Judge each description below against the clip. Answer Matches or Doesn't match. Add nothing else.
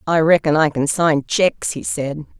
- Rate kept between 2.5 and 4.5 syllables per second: Doesn't match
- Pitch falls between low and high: Matches